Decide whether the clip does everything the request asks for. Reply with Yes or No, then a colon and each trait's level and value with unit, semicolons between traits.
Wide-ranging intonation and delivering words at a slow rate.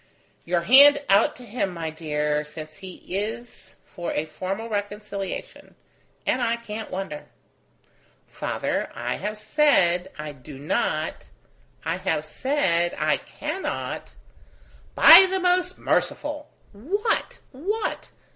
Yes: wide, 7.9 semitones; slow, 120 wpm